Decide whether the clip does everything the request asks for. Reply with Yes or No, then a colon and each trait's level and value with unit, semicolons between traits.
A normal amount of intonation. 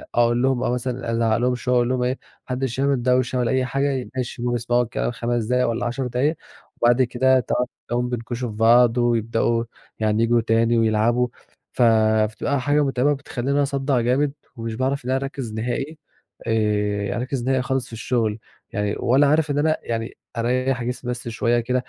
No: narrow, 2.1 semitones